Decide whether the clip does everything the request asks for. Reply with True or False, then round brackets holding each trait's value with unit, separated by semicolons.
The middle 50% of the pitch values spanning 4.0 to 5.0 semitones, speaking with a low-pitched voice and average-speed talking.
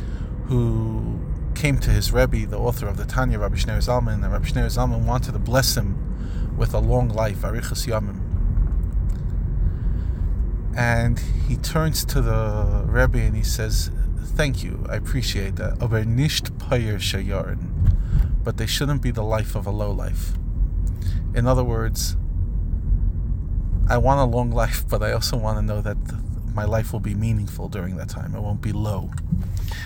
True (4.3 semitones; 105 Hz; 160 wpm)